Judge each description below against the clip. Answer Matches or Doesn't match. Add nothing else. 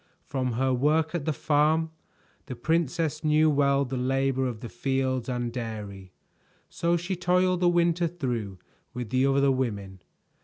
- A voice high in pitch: Doesn't match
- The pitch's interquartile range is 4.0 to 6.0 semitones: Matches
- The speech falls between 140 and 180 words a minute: Matches